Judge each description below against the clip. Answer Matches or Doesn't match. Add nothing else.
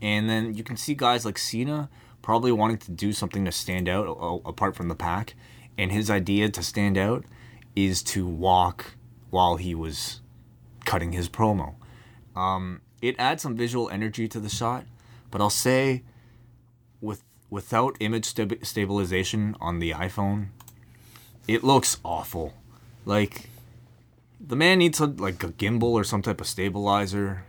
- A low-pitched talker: Matches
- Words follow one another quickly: Doesn't match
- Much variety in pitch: Doesn't match